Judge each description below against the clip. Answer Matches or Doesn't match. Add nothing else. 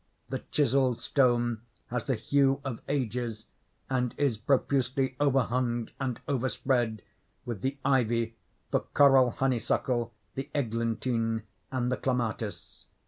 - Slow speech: Matches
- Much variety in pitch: Doesn't match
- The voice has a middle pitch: Doesn't match